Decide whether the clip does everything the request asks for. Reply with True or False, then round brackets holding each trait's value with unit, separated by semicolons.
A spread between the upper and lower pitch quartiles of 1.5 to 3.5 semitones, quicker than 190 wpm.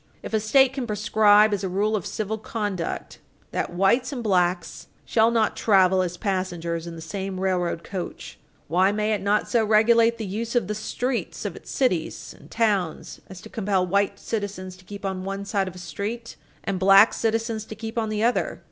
True (3.0 semitones; 200 wpm)